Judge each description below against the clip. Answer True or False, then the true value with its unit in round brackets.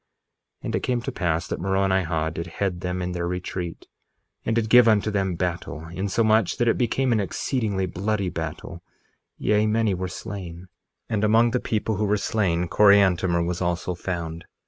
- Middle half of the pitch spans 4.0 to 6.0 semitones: False (3.6 semitones)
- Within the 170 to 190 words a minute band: True (175 wpm)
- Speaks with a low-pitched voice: True (95 Hz)